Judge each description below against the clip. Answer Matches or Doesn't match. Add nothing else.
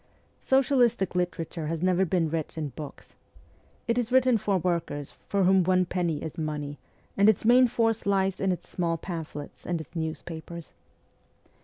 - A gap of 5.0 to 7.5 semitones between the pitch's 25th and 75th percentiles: Doesn't match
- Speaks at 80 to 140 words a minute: Doesn't match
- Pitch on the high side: Doesn't match